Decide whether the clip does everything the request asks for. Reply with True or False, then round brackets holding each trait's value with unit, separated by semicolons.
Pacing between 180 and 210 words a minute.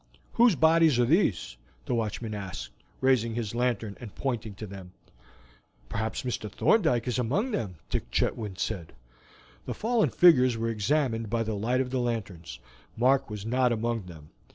False (160 wpm)